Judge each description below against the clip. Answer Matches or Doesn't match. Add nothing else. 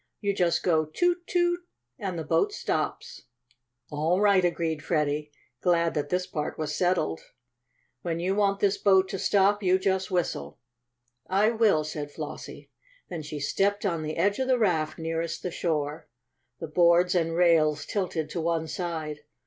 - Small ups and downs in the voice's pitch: Doesn't match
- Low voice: Doesn't match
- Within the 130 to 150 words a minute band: Doesn't match